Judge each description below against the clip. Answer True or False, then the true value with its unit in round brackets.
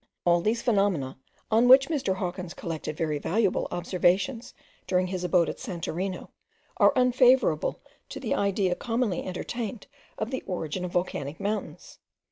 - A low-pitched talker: False (190 Hz)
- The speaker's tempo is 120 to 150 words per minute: True (140 wpm)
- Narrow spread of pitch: False (4.6 semitones)